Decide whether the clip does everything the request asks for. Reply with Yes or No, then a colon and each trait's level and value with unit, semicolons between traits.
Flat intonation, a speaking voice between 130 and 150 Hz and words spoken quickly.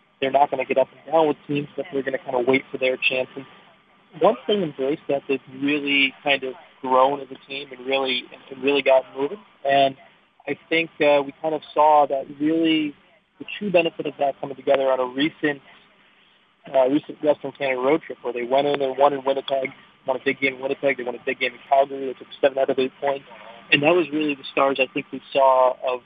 Yes: narrow, 1.7 semitones; low, 135 Hz; fast, 240 wpm